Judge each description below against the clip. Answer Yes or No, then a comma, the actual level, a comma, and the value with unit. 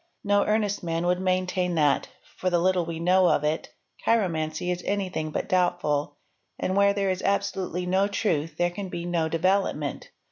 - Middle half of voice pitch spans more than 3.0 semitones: No, average, 2.7 semitones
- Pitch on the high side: No, medium, 180 Hz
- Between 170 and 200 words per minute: Yes, average, 185 wpm